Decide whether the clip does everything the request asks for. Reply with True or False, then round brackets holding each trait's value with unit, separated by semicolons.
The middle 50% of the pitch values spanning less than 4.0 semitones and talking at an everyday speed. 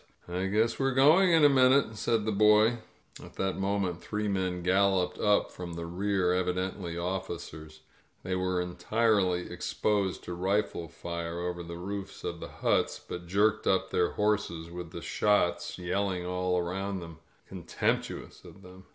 True (2.8 semitones; 155 wpm)